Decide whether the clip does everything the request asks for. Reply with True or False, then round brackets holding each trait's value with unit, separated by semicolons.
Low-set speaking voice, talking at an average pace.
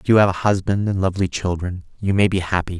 False (95 Hz; 260 wpm)